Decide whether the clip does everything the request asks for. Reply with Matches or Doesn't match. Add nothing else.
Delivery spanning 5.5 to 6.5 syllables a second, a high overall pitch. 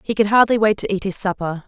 Matches